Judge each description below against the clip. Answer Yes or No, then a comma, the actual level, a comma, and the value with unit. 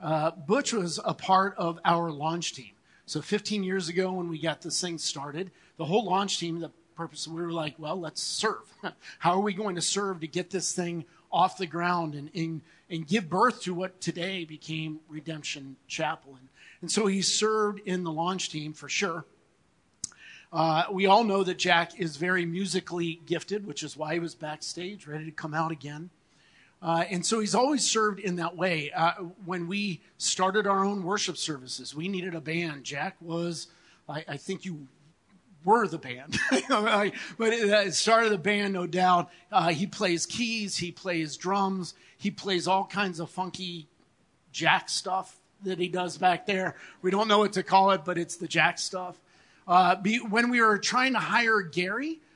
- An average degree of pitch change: Yes, average, 3.0 semitones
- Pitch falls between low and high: Yes, medium, 180 Hz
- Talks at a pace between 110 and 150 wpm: No, average, 190 wpm